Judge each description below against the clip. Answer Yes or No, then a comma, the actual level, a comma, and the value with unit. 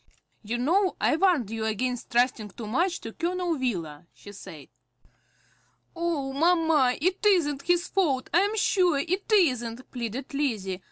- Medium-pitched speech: No, very high, 280 Hz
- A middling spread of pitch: No, wide, 7.0 semitones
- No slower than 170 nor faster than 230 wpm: No, average, 150 wpm